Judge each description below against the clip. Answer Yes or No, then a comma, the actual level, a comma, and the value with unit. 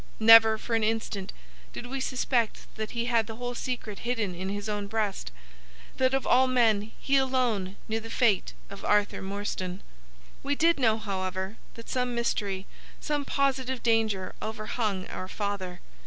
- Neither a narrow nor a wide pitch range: Yes, average, 3.7 semitones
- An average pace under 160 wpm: Yes, average, 150 wpm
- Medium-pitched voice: No, high, 220 Hz